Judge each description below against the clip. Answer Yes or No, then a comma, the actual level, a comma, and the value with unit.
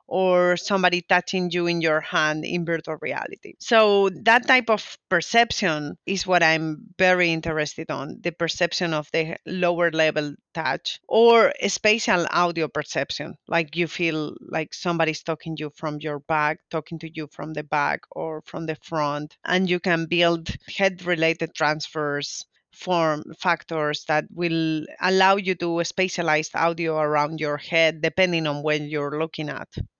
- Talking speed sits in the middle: Yes, average, 150 wpm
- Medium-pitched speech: Yes, medium, 165 Hz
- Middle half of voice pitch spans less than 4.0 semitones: Yes, narrow, 2.6 semitones